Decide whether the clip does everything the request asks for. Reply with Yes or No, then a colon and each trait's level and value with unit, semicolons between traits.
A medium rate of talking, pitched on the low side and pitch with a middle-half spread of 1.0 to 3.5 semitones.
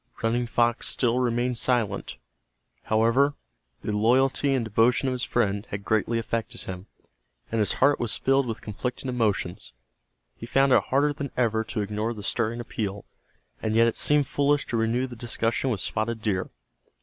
Yes: average, 170 wpm; low, 115 Hz; average, 2.7 semitones